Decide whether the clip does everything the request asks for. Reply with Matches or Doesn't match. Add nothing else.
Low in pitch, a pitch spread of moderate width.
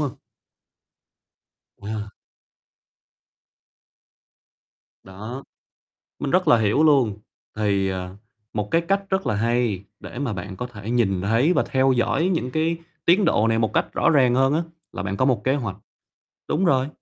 Doesn't match